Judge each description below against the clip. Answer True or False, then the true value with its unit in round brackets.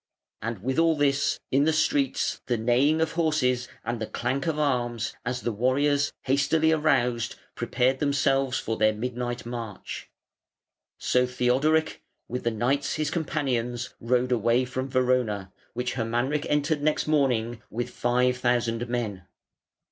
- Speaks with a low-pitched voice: True (125 Hz)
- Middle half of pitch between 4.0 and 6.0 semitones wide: False (3.1 semitones)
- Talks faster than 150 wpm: False (140 wpm)